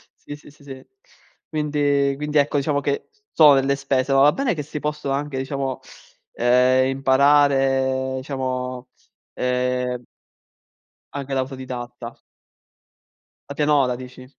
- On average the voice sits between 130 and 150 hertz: Yes, low, 135 Hz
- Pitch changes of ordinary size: No, narrow, 1.9 semitones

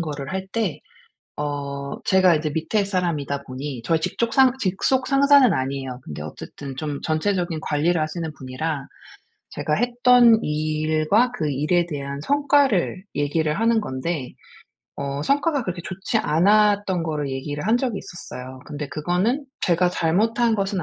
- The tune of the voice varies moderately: No, wide, 6.4 semitones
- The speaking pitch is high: No, medium, 170 Hz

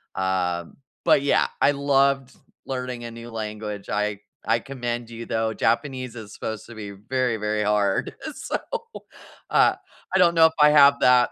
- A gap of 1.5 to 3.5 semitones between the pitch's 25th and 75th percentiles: No, average, 4.3 semitones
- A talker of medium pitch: No, low, 115 Hz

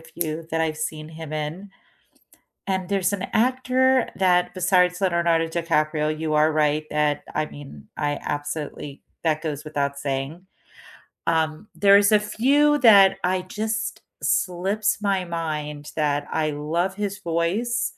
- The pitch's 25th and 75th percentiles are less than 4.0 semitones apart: No, average, 4.3 semitones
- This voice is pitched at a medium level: Yes, medium, 165 Hz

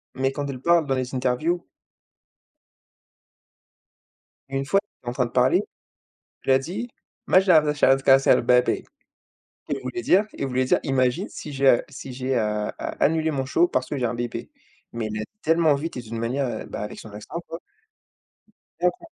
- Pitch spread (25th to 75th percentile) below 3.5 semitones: No, average, 4.3 semitones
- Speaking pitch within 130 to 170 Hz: Yes, low, 135 Hz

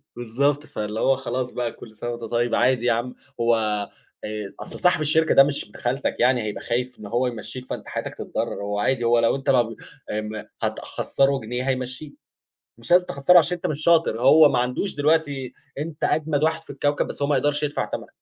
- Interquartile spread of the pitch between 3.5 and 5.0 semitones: Yes, average, 3.8 semitones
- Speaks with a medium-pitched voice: No, low, 130 Hz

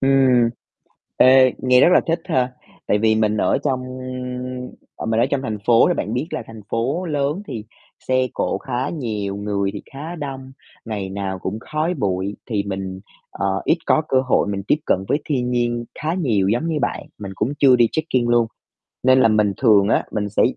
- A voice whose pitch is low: Yes, low, 120 Hz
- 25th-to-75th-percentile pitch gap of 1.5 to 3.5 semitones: No, average, 4.5 semitones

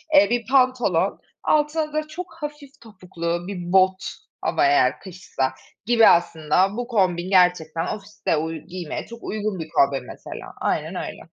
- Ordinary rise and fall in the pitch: No, wide, 6.8 semitones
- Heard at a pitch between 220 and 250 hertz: No, high, 195 Hz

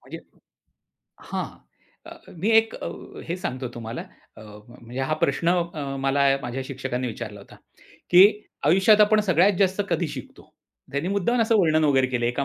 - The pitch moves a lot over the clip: Yes, wide, 7.0 semitones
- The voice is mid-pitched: Yes, medium, 155 Hz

